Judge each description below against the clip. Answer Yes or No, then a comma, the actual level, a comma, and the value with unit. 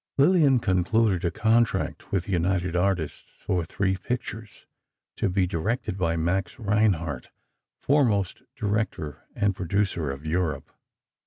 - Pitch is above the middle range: No, very low, 95 Hz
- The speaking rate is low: Yes, slow, 125 wpm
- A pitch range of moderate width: Yes, average, 4.1 semitones